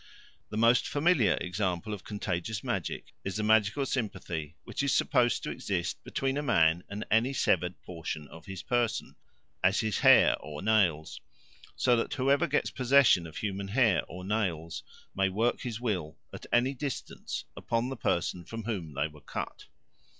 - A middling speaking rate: Yes, average, 165 wpm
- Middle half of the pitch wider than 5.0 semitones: Yes, wide, 5.6 semitones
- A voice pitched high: No, low, 105 Hz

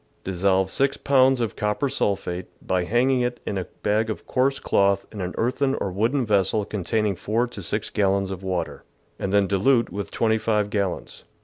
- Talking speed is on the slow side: No, average, 185 wpm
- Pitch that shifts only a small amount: No, average, 3.7 semitones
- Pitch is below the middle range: Yes, low, 105 Hz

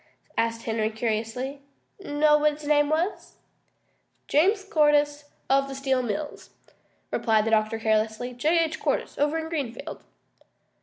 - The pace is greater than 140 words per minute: No, slow, 135 wpm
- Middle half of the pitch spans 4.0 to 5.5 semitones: Yes, average, 4.9 semitones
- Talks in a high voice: Yes, very high, 280 Hz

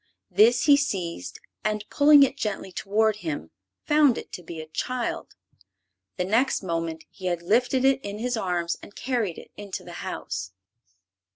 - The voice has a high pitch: Yes, high, 205 Hz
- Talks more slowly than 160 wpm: No, average, 165 wpm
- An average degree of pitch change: No, wide, 6.2 semitones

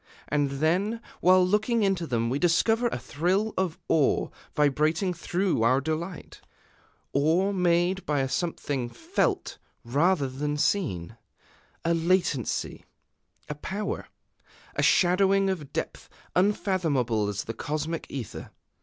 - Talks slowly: Yes, slow, 120 wpm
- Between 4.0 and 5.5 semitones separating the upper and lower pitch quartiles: Yes, average, 5.1 semitones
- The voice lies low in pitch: No, medium, 165 Hz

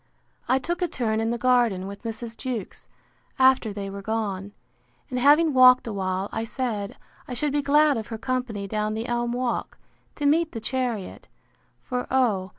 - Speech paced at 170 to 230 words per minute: Yes, average, 180 wpm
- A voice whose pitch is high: Yes, high, 240 Hz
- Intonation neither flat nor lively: Yes, average, 3.4 semitones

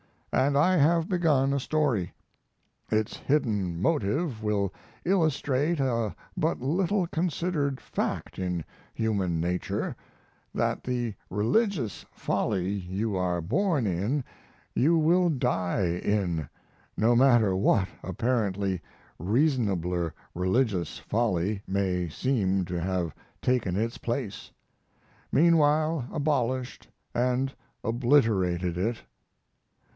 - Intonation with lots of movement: Yes, wide, 7.2 semitones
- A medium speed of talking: No, slow, 100 wpm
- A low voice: Yes, low, 115 Hz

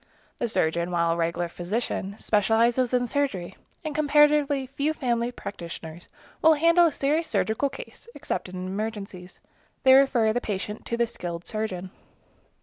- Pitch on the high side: Yes, high, 225 Hz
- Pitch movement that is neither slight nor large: No, wide, 7.1 semitones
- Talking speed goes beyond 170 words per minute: No, average, 145 wpm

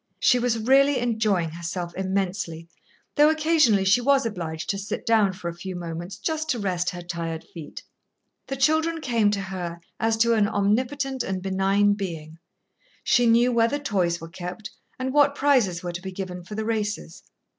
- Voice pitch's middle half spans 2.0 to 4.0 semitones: No, wide, 5.5 semitones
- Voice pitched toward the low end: No, high, 205 Hz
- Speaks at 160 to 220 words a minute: Yes, average, 180 wpm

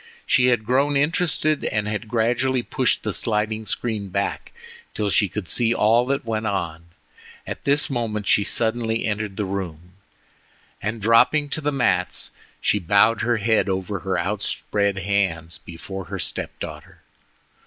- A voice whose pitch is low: Yes, low, 110 Hz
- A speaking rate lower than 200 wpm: Yes, average, 155 wpm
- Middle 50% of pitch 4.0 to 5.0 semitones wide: No, average, 3.3 semitones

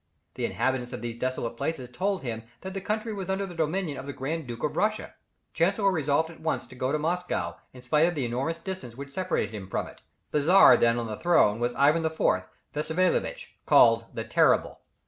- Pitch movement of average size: No, wide, 6.3 semitones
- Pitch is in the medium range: Yes, medium, 150 Hz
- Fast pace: Yes, fast, 210 wpm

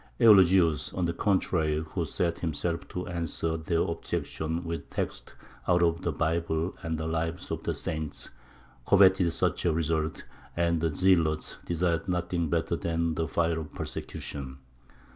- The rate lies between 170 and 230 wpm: No, average, 150 wpm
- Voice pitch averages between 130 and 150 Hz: No, very low, 85 Hz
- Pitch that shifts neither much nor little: No, narrow, 1.5 semitones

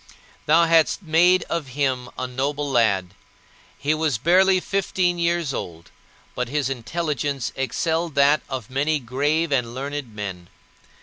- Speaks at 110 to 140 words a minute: Yes, slow, 135 wpm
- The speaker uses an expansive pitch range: No, average, 4.6 semitones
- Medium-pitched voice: Yes, medium, 145 Hz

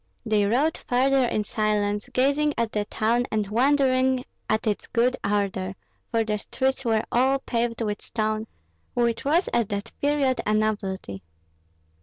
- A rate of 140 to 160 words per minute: Yes, average, 150 wpm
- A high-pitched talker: Yes, high, 230 Hz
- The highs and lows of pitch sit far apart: No, average, 3.6 semitones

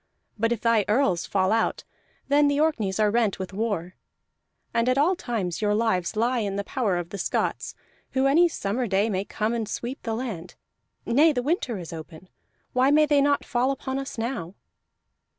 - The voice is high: Yes, high, 230 Hz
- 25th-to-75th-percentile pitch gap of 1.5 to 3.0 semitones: No, average, 5.1 semitones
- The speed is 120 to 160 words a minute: No, average, 190 wpm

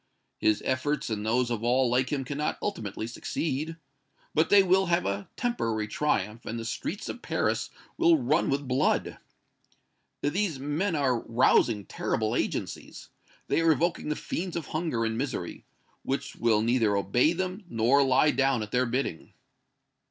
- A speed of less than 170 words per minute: Yes, average, 160 wpm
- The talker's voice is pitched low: Yes, low, 130 Hz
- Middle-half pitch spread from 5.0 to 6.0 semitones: Yes, wide, 5.5 semitones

